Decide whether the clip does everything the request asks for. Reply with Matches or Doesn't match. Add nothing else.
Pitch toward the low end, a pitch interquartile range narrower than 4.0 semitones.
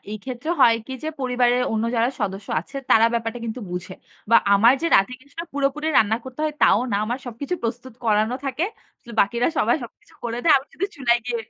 Doesn't match